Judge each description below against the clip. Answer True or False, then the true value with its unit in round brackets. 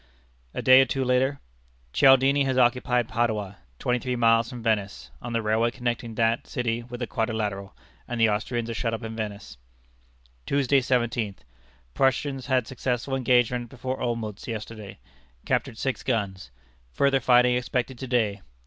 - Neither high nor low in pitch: False (120 Hz)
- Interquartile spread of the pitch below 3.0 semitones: True (2.4 semitones)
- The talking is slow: False (155 wpm)